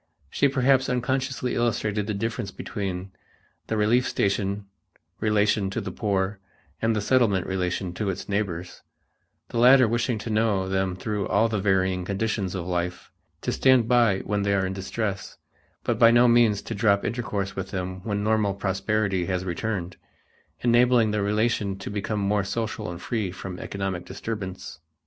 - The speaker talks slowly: No, average, 165 wpm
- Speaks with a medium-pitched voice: No, low, 105 Hz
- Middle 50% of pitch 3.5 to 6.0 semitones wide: No, average, 3.0 semitones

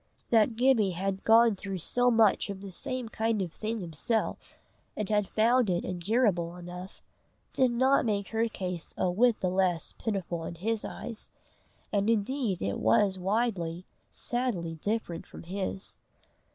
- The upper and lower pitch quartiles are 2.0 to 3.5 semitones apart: No, average, 4.1 semitones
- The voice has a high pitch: Yes, high, 200 Hz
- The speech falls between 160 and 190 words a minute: No, average, 150 wpm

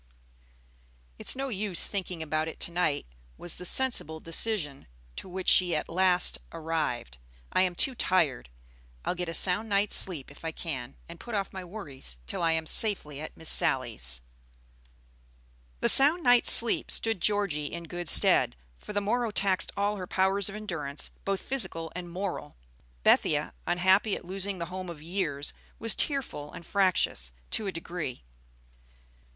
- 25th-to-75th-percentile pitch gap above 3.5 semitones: Yes, average, 4.1 semitones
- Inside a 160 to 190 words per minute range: Yes, average, 165 wpm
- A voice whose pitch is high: No, medium, 180 Hz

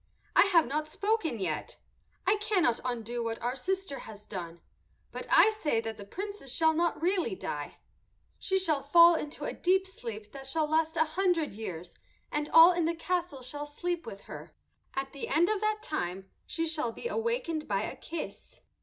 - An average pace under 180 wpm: No, average, 185 wpm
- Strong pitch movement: Yes, wide, 7.2 semitones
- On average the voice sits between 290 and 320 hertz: Yes, very high, 310 Hz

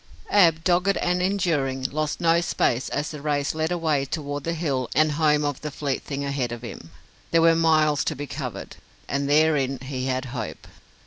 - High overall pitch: No, medium, 150 Hz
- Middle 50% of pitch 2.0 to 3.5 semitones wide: Yes, average, 2.9 semitones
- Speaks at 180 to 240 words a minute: Yes, average, 190 wpm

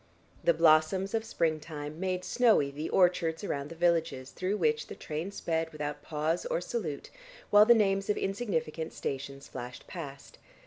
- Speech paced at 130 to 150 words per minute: No, average, 160 wpm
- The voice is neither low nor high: Yes, medium, 165 Hz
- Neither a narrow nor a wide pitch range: Yes, average, 4.4 semitones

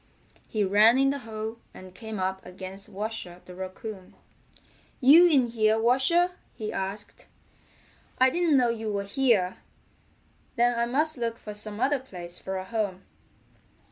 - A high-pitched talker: Yes, high, 220 Hz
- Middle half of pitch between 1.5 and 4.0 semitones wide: No, average, 4.6 semitones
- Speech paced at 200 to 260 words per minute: No, average, 150 wpm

